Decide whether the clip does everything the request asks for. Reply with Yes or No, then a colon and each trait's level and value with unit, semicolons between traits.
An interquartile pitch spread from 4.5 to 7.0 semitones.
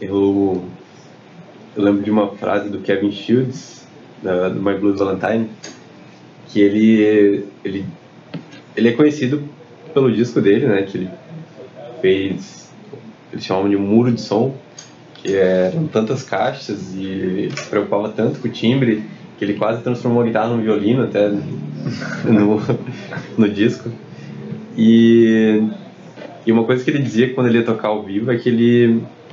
No: average, 3.0 semitones